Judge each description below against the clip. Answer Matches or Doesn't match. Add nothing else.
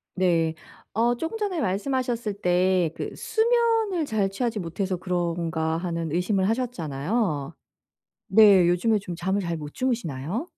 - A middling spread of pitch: Doesn't match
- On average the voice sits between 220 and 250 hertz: Doesn't match